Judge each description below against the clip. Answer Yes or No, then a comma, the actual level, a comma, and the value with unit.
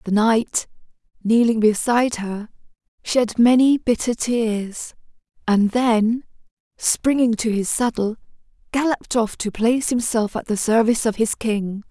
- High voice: Yes, high, 225 Hz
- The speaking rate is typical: No, slow, 130 wpm